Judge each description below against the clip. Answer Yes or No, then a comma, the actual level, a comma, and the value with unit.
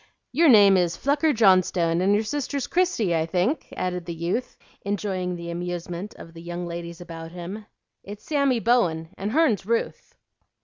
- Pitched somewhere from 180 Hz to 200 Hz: Yes, medium, 185 Hz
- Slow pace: No, average, 165 wpm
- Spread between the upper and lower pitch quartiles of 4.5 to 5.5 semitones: Yes, average, 5.2 semitones